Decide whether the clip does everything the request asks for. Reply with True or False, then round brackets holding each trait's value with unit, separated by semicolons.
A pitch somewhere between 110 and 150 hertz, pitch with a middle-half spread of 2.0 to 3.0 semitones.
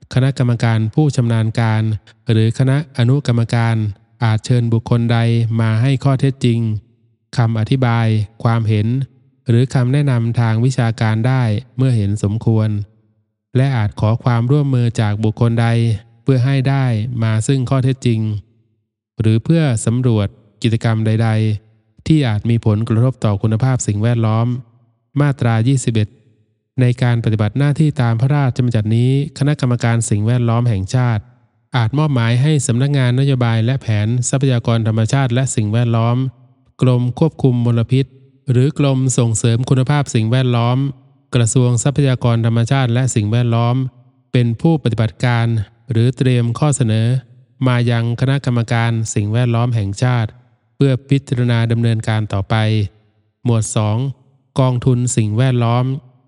True (120 Hz; 2.5 semitones)